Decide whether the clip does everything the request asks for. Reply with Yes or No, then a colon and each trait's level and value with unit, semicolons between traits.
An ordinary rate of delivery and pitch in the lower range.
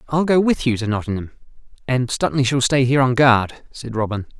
Yes: average, 190 wpm; low, 130 Hz